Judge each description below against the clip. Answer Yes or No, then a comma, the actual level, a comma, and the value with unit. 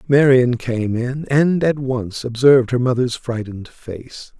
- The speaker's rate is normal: Yes, average, 150 wpm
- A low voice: Yes, low, 125 Hz